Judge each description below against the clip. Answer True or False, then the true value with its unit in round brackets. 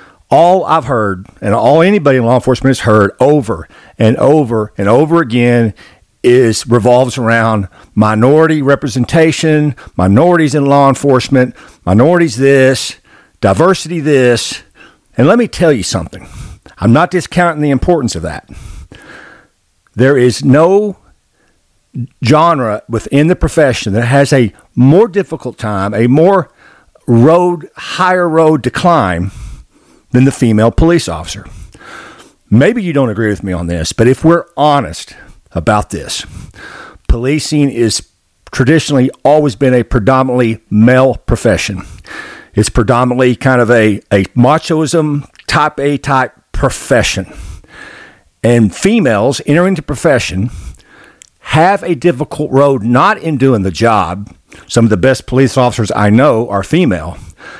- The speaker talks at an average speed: False (130 wpm)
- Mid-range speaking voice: False (130 Hz)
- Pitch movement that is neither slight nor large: True (5.0 semitones)